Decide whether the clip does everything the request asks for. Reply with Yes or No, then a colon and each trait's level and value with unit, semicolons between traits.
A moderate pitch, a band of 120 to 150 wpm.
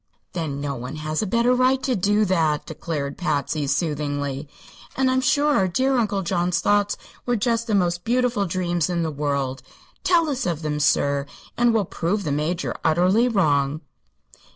No: medium, 175 Hz; average, 175 wpm